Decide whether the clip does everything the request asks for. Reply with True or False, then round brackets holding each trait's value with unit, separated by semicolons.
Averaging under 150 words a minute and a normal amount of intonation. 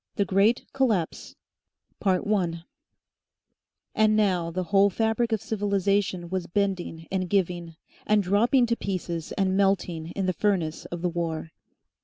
True (135 wpm; 3.0 semitones)